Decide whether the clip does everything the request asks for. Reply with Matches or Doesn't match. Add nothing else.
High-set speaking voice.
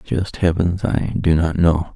Doesn't match